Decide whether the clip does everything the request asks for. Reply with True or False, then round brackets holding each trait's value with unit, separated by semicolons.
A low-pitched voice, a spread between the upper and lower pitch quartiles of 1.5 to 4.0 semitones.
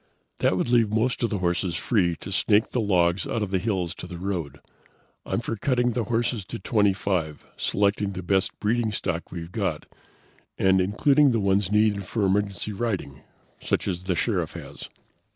True (100 Hz; 3.4 semitones)